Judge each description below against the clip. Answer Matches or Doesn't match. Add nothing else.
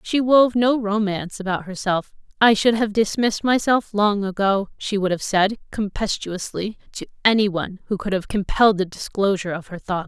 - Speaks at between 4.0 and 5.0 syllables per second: Doesn't match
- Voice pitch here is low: Doesn't match